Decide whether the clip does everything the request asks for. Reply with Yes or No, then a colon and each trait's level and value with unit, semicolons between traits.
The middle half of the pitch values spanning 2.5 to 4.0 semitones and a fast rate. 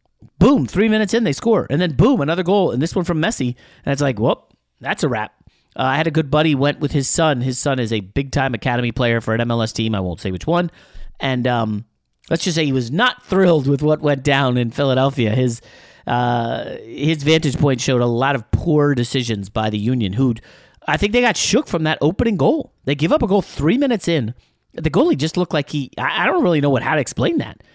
No: average, 4.8 semitones; fast, 240 wpm